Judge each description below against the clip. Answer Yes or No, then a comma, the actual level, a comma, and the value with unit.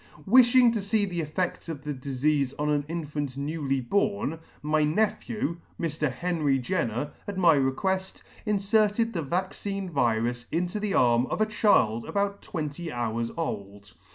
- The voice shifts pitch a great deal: Yes, wide, 6.4 semitones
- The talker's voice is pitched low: No, medium, 160 Hz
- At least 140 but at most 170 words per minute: Yes, average, 150 wpm